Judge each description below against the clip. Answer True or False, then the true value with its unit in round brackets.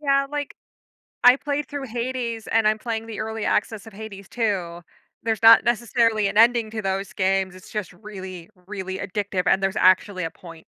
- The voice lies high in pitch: True (215 Hz)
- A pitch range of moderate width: True (3.2 semitones)